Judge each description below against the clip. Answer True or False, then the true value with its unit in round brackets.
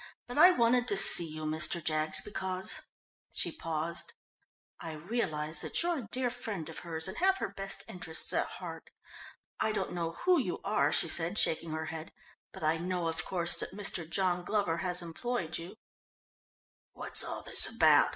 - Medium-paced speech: True (180 wpm)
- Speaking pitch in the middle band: True (175 Hz)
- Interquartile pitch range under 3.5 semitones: False (4.4 semitones)